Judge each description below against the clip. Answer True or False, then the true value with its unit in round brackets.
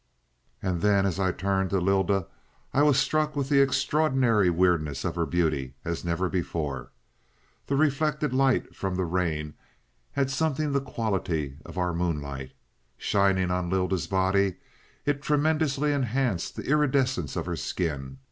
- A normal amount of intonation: False (8.0 semitones)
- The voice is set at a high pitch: False (95 Hz)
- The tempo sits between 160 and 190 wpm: False (145 wpm)